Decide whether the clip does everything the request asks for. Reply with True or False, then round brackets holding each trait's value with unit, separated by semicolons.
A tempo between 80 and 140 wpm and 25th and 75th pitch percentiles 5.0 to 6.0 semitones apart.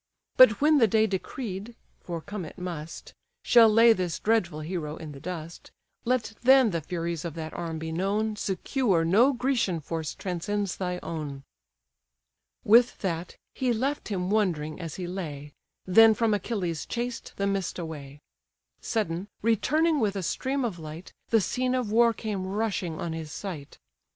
False (160 wpm; 5.3 semitones)